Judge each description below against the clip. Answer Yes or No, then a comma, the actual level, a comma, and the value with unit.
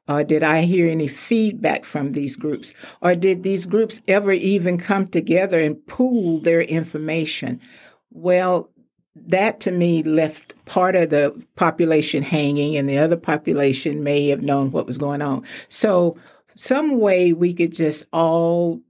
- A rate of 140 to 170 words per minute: Yes, average, 160 wpm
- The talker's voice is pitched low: No, medium, 165 Hz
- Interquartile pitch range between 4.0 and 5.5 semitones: No, average, 3.4 semitones